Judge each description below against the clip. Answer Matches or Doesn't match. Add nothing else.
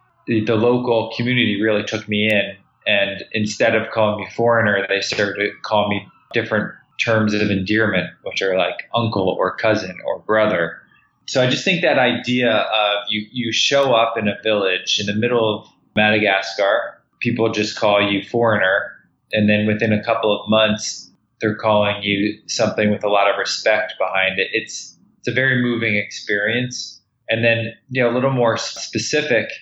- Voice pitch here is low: Matches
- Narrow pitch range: Matches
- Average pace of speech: Matches